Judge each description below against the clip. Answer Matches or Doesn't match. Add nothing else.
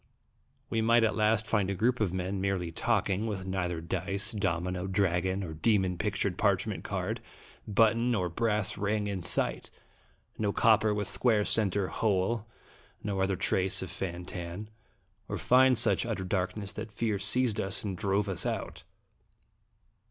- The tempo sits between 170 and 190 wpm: Doesn't match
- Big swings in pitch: Doesn't match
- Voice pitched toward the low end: Matches